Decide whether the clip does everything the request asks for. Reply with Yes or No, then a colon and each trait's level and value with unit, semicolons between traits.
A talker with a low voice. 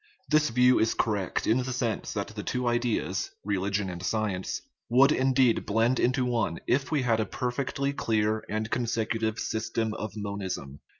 Yes: low, 115 Hz